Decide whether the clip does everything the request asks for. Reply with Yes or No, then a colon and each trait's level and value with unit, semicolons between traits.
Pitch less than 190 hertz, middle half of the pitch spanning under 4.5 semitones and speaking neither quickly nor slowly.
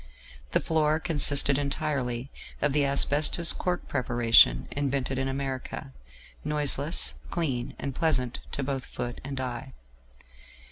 No: medium, 140 Hz; average, 2.8 semitones; slow, 120 wpm